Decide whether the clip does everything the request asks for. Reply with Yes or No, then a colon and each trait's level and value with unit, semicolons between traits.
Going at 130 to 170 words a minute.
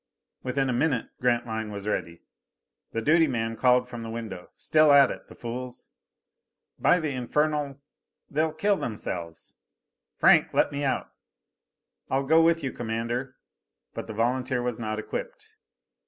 Yes: average, 145 wpm